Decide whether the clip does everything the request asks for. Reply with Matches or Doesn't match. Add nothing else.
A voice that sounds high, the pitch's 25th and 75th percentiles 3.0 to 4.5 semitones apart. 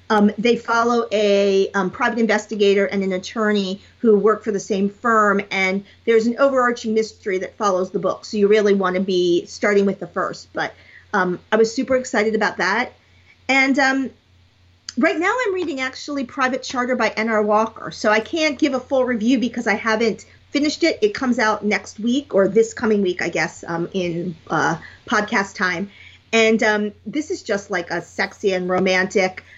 Matches